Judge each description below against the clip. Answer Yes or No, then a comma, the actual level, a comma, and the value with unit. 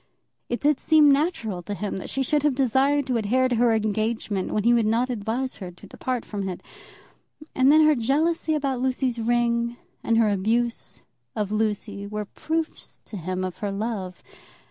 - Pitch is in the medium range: No, high, 235 Hz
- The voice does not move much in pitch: No, average, 4.1 semitones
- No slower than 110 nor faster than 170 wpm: No, average, 185 wpm